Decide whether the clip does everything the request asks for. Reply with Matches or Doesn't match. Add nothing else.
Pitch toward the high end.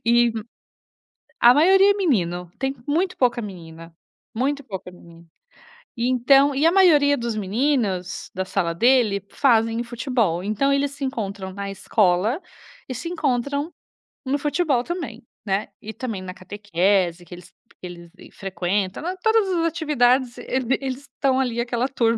Matches